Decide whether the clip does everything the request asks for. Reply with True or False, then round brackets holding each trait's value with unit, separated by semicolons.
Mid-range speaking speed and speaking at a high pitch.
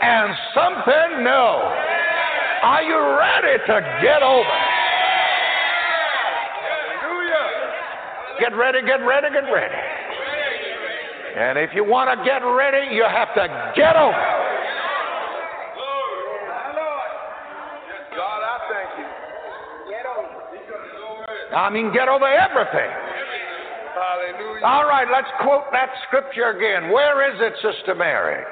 False (95 wpm; 270 Hz)